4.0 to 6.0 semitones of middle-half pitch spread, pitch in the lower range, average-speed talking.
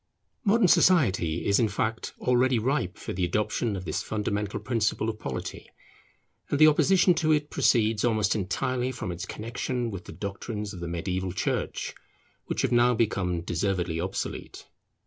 Yes: average, 5.1 semitones; low, 105 Hz; average, 160 wpm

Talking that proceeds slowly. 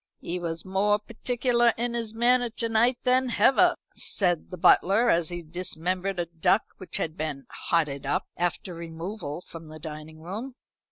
No: average, 165 wpm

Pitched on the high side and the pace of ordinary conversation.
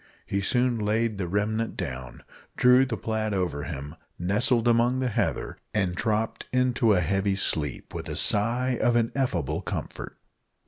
No: low, 110 Hz; average, 150 wpm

